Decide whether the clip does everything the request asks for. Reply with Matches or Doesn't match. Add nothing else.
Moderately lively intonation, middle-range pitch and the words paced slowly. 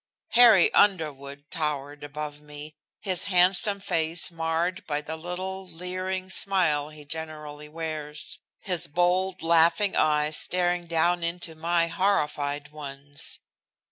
Matches